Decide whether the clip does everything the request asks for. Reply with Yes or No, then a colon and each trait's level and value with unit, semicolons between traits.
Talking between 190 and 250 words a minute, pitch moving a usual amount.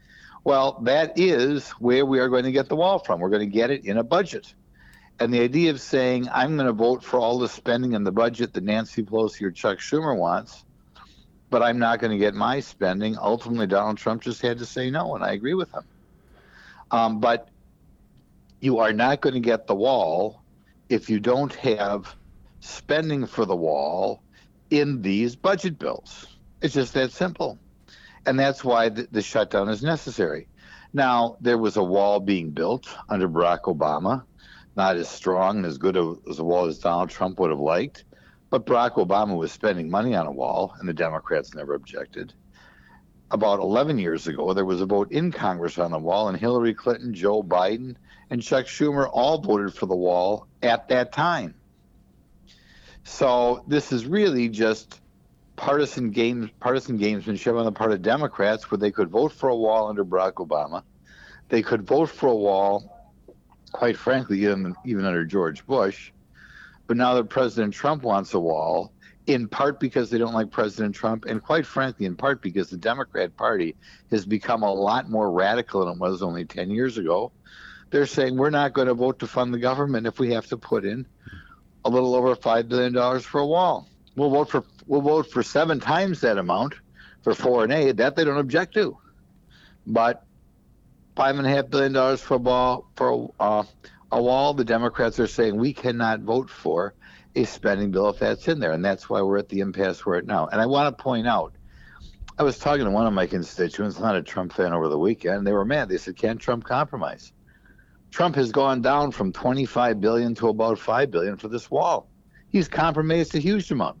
Yes: average, 195 wpm; average, 4.3 semitones